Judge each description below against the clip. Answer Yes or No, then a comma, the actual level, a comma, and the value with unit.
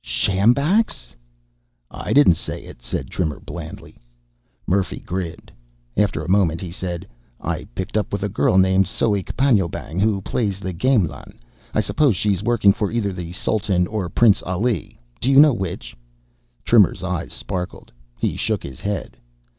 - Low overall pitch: Yes, very low, 95 Hz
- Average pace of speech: Yes, average, 155 wpm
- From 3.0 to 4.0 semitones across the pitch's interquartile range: Yes, average, 3.4 semitones